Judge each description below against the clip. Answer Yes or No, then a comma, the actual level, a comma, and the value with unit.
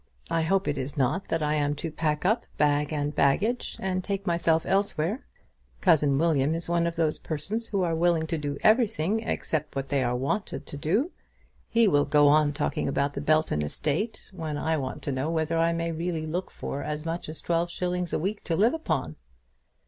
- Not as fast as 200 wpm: No, fast, 205 wpm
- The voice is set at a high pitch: No, medium, 160 Hz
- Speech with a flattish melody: No, average, 3.5 semitones